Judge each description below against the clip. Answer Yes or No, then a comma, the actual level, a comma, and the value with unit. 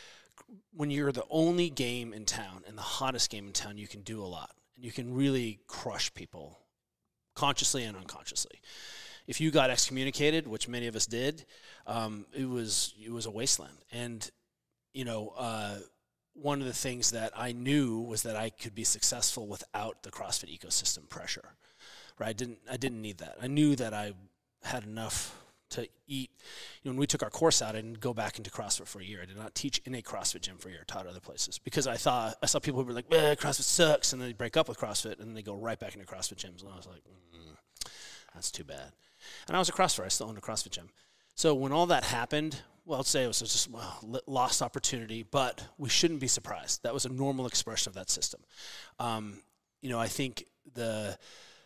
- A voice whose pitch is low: Yes, low, 120 Hz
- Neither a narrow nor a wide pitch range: Yes, average, 4.0 semitones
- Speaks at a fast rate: Yes, fast, 225 wpm